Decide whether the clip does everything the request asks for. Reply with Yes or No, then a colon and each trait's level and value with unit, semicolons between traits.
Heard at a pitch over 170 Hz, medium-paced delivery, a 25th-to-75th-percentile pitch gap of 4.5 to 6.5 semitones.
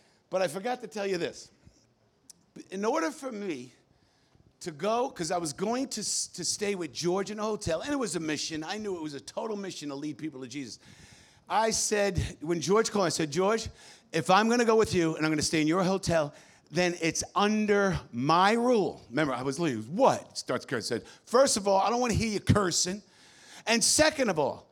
No: medium, 185 Hz; fast, 220 wpm; average, 4.9 semitones